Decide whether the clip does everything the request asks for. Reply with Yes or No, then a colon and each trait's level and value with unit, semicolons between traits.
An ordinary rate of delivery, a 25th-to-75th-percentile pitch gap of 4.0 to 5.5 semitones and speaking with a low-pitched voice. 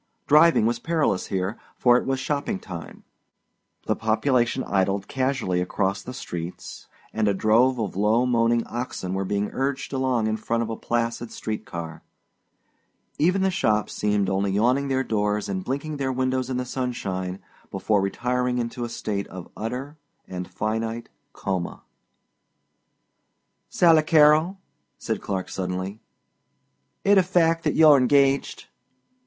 Yes: average, 145 wpm; average, 4.9 semitones; low, 115 Hz